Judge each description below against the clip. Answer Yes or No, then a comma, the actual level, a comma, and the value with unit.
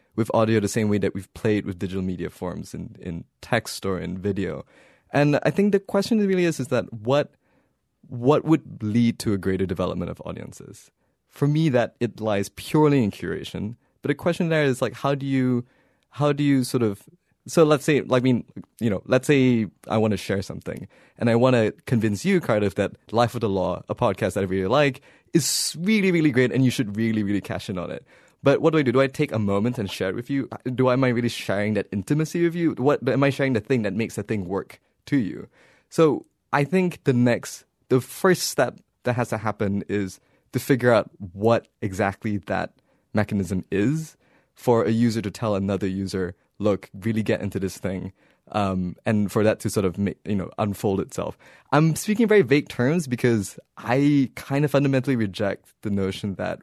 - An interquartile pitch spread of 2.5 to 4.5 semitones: No, wide, 5.5 semitones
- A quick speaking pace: Yes, fast, 215 wpm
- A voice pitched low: Yes, low, 115 Hz